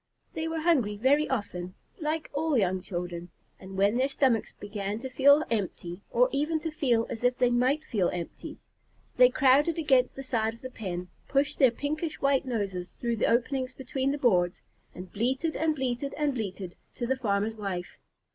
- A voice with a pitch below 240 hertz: No, very high, 250 Hz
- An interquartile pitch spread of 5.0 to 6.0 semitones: Yes, wide, 5.5 semitones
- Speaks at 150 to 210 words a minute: Yes, average, 185 wpm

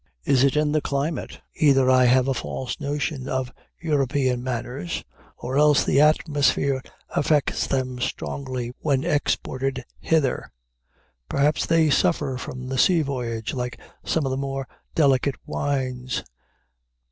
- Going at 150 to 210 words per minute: No, slow, 135 wpm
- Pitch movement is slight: Yes, narrow, 2.3 semitones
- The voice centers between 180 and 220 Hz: No, low, 135 Hz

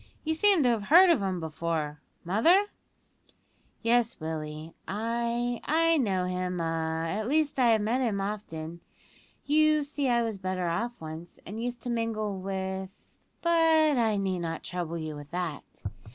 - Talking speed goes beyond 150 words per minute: Yes, average, 165 wpm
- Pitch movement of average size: No, wide, 6.3 semitones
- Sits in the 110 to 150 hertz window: No, high, 210 Hz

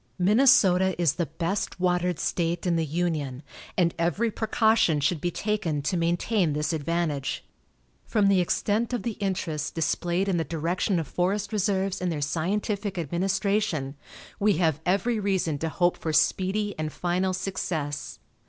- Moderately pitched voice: Yes, medium, 180 Hz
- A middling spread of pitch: Yes, average, 3.5 semitones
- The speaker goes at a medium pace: Yes, average, 155 wpm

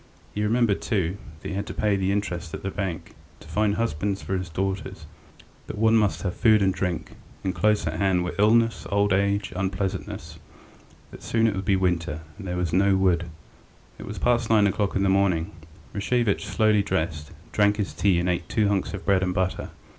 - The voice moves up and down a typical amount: No, narrow, 2.3 semitones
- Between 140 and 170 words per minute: No, fast, 205 wpm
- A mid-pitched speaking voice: No, very low, 95 Hz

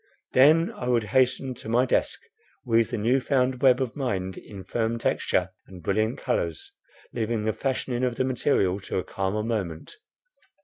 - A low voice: Yes, low, 115 Hz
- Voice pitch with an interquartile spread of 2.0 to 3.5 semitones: No, average, 4.2 semitones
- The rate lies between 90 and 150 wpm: No, average, 170 wpm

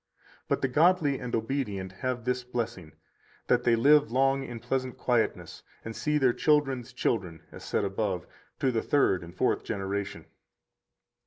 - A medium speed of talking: Yes, average, 155 wpm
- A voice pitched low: Yes, low, 125 Hz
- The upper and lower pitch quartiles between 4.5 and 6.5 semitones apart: Yes, average, 4.8 semitones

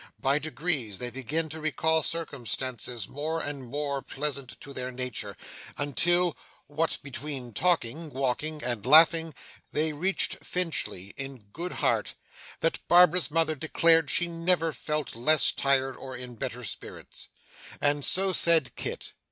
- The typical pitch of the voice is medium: Yes, medium, 145 Hz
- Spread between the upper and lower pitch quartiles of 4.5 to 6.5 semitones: No, average, 4.0 semitones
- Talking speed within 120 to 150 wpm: Yes, average, 140 wpm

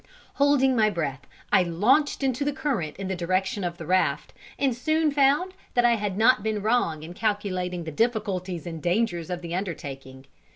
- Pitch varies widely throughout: Yes, wide, 6.1 semitones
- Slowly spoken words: No, average, 180 wpm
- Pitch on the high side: Yes, high, 200 Hz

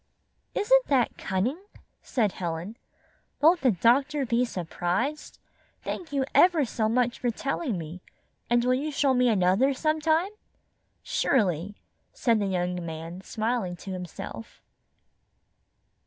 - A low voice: No, high, 235 Hz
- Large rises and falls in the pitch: Yes, wide, 7.3 semitones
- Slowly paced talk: Yes, slow, 125 wpm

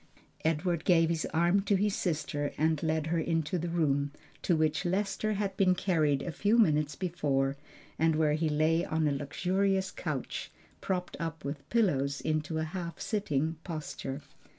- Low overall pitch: No, medium, 160 Hz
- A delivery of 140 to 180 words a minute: Yes, average, 165 wpm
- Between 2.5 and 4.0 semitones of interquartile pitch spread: Yes, average, 3.2 semitones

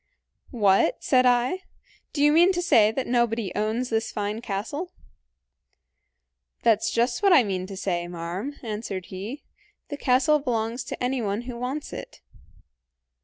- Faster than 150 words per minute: No, average, 145 wpm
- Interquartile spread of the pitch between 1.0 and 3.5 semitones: No, average, 4.1 semitones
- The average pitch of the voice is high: Yes, high, 235 Hz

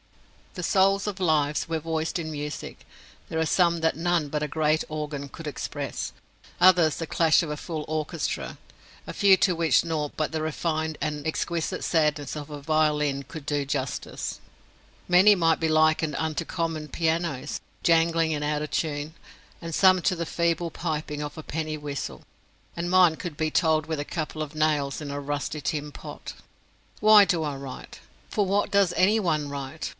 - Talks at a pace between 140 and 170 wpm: No, average, 180 wpm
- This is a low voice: No, medium, 155 Hz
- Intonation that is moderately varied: No, narrow, 2.2 semitones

